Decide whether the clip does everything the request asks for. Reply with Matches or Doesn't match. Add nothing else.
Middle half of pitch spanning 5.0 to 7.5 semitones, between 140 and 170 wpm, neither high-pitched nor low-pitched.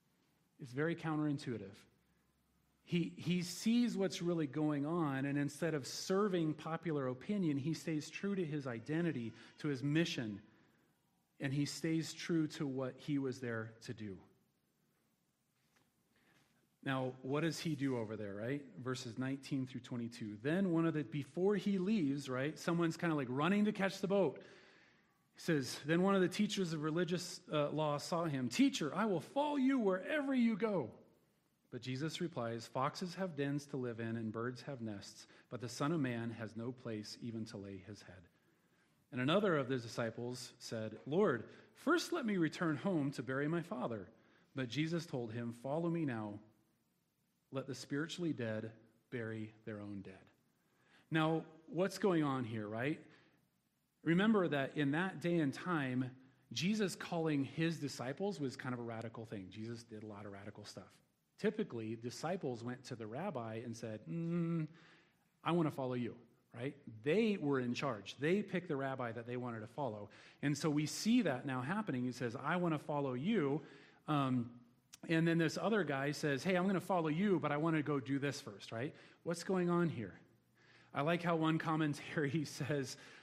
Doesn't match